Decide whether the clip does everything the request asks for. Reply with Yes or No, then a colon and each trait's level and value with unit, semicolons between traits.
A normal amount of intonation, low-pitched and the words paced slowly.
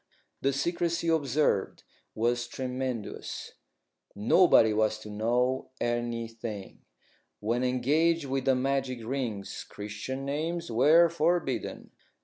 Yes: average, 4.1 semitones; low, 130 Hz; slow, 100 wpm